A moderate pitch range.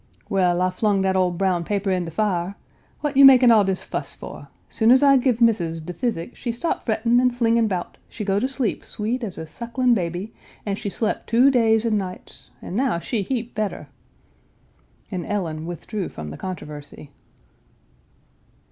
Yes: average, 4.7 semitones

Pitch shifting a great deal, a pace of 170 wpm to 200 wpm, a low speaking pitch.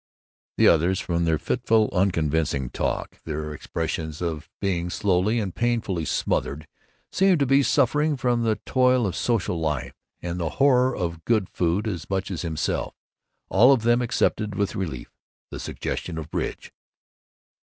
No: wide, 6.5 semitones; average, 150 wpm; very low, 95 Hz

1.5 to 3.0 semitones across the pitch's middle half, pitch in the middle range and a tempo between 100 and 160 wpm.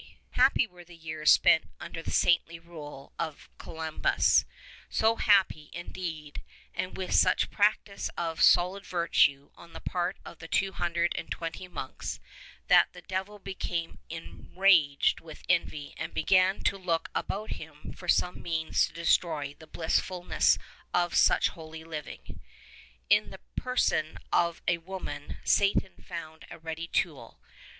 Yes: narrow, 2.5 semitones; medium, 170 Hz; average, 145 wpm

